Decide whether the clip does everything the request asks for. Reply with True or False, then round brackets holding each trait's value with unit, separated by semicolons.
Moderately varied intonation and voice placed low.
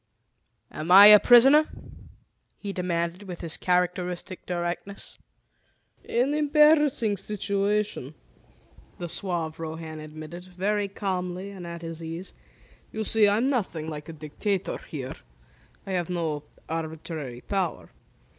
False (3.8 semitones; 180 Hz)